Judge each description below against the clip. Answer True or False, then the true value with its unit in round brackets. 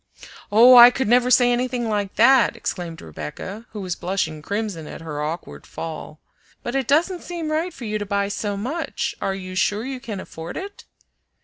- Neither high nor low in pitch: False (215 Hz)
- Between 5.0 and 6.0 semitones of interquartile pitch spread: True (5.5 semitones)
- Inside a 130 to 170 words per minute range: False (190 wpm)